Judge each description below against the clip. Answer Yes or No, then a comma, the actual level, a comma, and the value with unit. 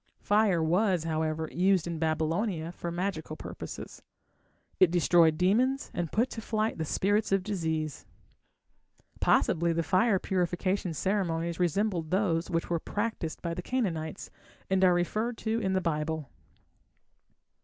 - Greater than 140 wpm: No, slow, 135 wpm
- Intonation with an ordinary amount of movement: Yes, average, 3.6 semitones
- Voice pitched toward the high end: No, medium, 175 Hz